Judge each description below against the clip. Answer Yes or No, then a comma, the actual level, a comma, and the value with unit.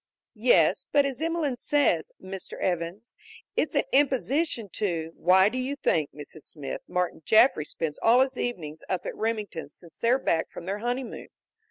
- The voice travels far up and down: Yes, wide, 7.4 semitones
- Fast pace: No, average, 170 wpm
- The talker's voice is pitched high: Yes, high, 210 Hz